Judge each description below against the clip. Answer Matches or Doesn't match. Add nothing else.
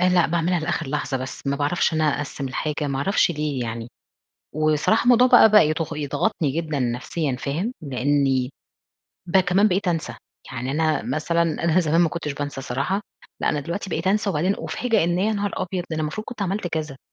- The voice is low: Doesn't match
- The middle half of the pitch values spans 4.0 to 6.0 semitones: Matches